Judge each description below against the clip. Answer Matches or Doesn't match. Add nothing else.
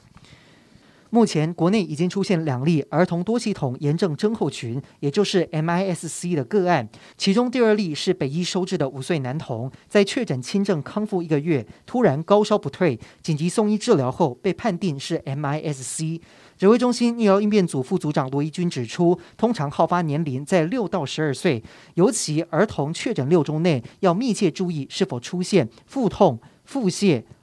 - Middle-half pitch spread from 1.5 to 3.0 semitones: Doesn't match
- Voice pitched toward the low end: Doesn't match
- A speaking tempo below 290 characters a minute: Matches